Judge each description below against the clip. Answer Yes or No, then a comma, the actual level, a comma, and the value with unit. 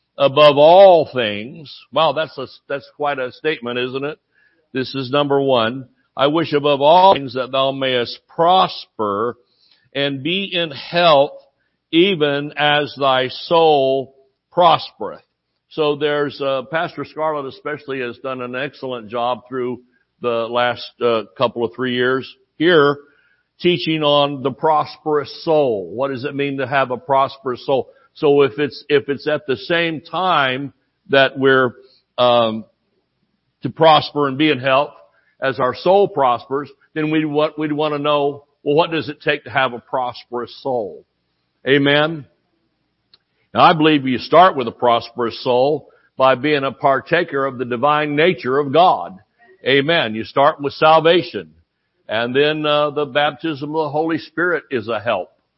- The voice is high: No, medium, 140 Hz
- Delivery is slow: No, average, 155 wpm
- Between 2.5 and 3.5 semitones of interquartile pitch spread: Yes, average, 2.8 semitones